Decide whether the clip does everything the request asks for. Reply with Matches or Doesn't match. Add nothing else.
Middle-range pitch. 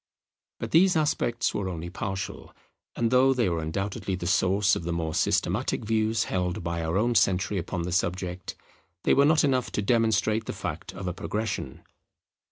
Doesn't match